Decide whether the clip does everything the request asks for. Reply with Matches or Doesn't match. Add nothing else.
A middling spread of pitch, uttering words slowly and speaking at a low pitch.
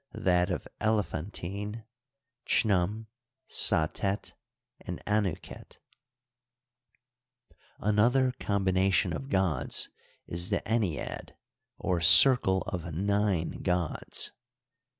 Matches